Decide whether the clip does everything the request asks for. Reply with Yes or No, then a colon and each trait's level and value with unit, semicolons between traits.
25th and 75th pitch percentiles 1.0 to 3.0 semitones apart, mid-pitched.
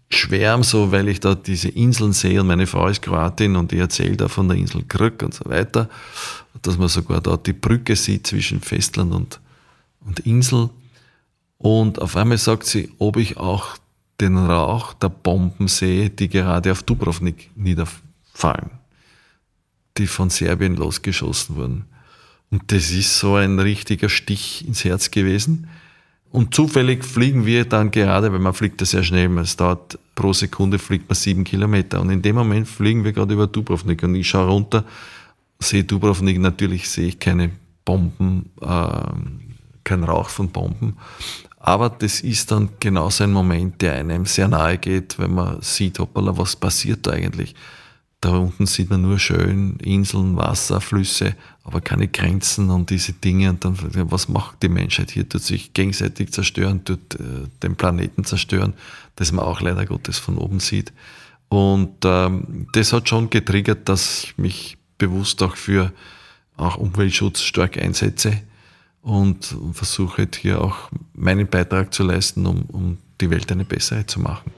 No: average, 2.7 semitones; very low, 95 Hz